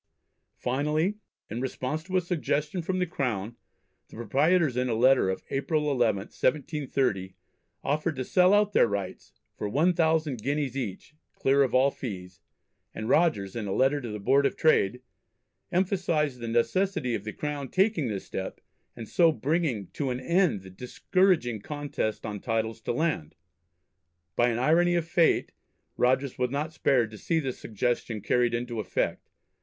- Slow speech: No, average, 165 wpm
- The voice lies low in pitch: Yes, low, 130 Hz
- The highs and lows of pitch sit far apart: Yes, wide, 5.7 semitones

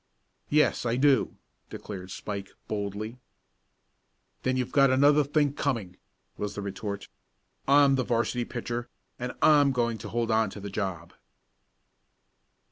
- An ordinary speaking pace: No, slow, 130 wpm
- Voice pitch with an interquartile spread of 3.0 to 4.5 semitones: No, average, 5.0 semitones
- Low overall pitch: Yes, low, 120 Hz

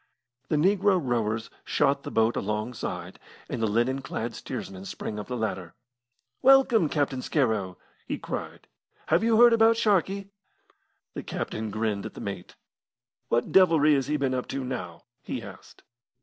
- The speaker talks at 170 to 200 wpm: No, average, 155 wpm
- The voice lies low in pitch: Yes, low, 130 Hz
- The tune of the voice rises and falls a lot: Yes, wide, 8.5 semitones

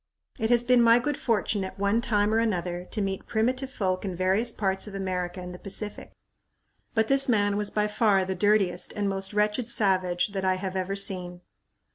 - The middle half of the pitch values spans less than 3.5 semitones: Yes, average, 2.9 semitones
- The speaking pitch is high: Yes, high, 200 Hz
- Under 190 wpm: No, average, 200 wpm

